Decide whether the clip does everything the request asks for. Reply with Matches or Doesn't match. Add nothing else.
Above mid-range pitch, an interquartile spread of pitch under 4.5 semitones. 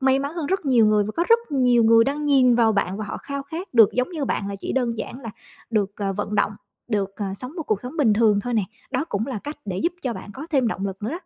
Doesn't match